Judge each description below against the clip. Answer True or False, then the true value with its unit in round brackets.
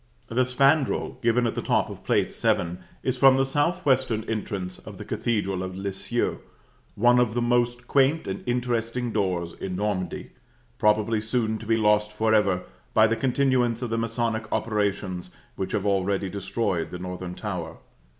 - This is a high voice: False (110 Hz)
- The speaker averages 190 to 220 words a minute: False (160 wpm)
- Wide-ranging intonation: False (3.8 semitones)